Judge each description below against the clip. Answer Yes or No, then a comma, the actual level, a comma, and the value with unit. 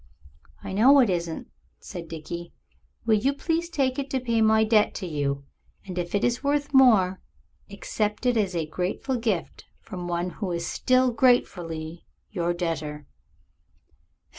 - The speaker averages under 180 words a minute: Yes, average, 155 wpm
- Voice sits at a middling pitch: No, high, 200 Hz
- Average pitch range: No, wide, 6.4 semitones